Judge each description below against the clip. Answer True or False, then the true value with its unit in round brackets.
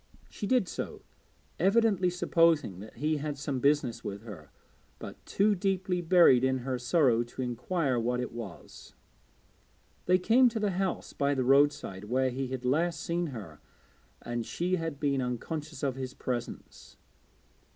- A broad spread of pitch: True (6.0 semitones)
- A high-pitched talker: False (140 Hz)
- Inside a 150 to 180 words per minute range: True (155 wpm)